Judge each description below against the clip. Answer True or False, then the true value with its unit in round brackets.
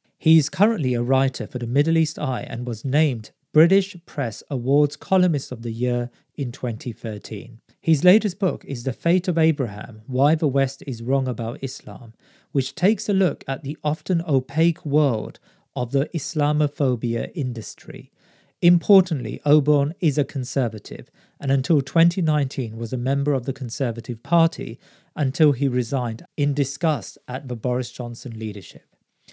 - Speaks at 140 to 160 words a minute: True (155 wpm)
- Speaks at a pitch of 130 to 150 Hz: True (140 Hz)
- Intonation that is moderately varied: True (4.1 semitones)